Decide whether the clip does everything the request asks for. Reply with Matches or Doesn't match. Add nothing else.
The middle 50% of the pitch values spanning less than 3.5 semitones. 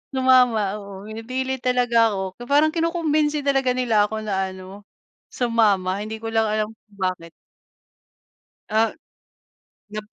Doesn't match